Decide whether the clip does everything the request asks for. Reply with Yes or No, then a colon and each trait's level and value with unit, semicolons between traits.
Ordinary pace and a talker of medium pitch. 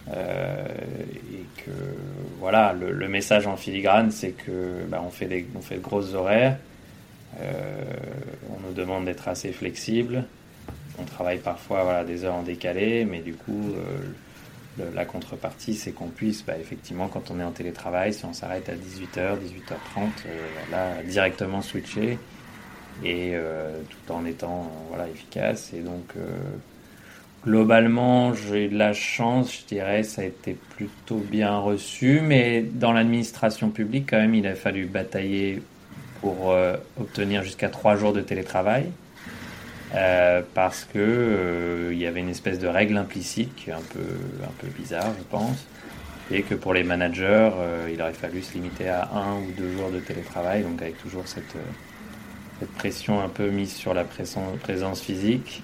No: average, 165 wpm; very low, 95 Hz